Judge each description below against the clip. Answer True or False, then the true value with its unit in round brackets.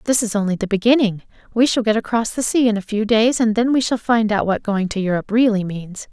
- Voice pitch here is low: False (220 Hz)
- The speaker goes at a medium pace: False (265 wpm)